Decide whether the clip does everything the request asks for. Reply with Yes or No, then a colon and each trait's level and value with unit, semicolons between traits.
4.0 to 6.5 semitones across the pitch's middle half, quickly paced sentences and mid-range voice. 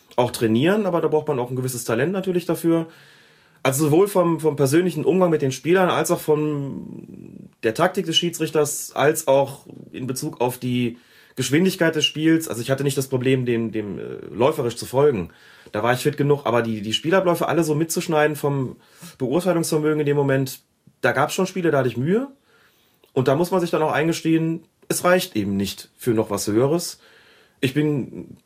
Yes: average, 4.7 semitones; fast, 195 wpm; medium, 150 Hz